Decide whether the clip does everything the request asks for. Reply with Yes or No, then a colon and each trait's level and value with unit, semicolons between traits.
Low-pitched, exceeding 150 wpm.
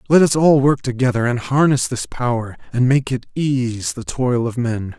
Yes: low, 125 Hz; fast, 205 wpm